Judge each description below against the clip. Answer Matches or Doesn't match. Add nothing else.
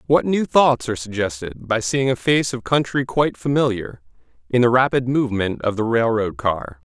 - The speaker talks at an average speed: Matches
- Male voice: Matches